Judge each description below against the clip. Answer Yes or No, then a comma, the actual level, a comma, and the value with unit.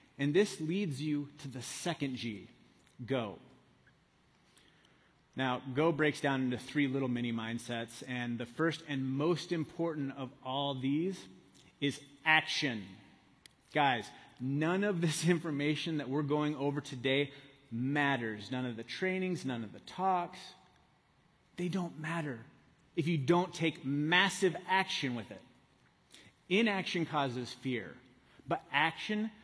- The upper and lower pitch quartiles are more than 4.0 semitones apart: Yes, average, 4.7 semitones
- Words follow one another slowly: Yes, slow, 130 wpm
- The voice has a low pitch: No, medium, 145 Hz